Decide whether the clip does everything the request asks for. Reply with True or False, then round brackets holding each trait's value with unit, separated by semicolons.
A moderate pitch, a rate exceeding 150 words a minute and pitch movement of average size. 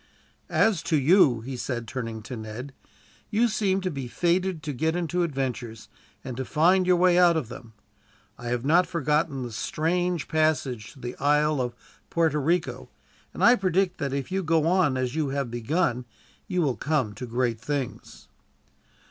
False (150 Hz; 175 wpm; 5.8 semitones)